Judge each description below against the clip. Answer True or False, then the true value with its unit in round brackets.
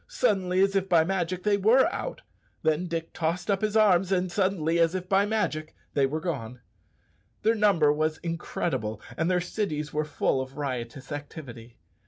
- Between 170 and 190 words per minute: True (175 wpm)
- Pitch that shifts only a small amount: False (4.3 semitones)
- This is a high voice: False (170 Hz)